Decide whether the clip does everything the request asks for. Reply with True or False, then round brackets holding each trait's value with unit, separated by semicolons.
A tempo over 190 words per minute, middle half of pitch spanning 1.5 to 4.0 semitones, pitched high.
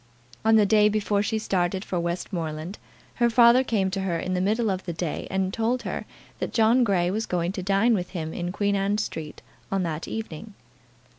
True (205 wpm; 3.6 semitones; 195 Hz)